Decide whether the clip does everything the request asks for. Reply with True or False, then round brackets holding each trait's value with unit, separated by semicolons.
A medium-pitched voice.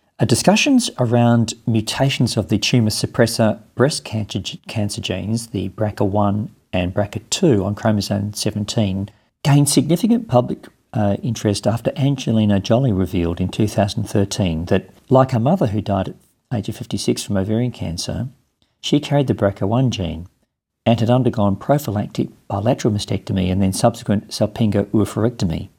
False (110 Hz)